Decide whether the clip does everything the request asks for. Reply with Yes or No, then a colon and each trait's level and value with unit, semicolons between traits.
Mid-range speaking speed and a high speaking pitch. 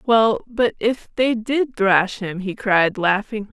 Yes: average, 170 wpm; high, 215 Hz